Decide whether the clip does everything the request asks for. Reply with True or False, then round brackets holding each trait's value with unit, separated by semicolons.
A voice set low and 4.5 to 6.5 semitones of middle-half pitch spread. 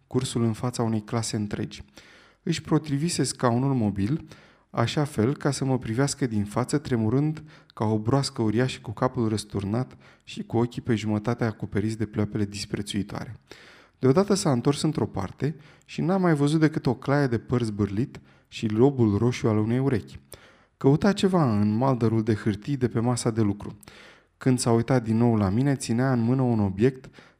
False (120 Hz; 3.8 semitones)